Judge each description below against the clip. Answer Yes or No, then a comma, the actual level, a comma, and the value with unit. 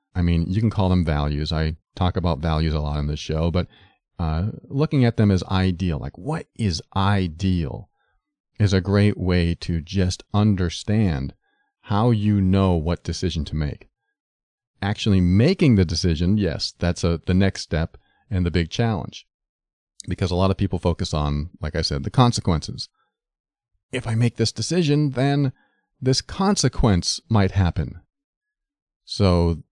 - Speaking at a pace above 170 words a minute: No, average, 160 wpm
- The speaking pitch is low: Yes, very low, 95 Hz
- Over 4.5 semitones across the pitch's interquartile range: Yes, average, 5.0 semitones